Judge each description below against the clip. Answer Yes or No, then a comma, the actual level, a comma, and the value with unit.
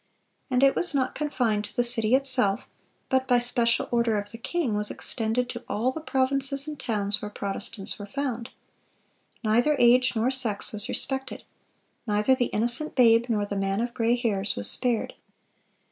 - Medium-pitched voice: No, high, 235 Hz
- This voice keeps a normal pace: Yes, average, 175 wpm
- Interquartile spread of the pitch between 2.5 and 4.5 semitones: Yes, average, 3.6 semitones